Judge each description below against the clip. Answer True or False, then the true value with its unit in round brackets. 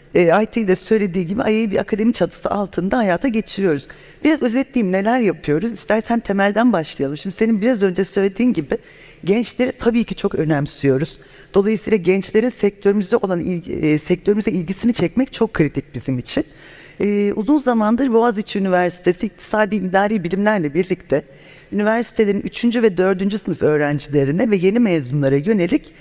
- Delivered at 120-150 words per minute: True (140 wpm)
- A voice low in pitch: False (200 Hz)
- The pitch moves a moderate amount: True (4.3 semitones)